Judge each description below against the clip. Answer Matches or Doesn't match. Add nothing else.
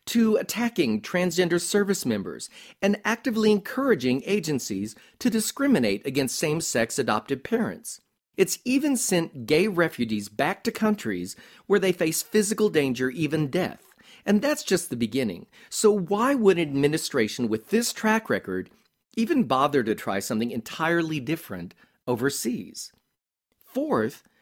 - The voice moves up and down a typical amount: Doesn't match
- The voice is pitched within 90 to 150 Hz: Doesn't match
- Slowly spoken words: Matches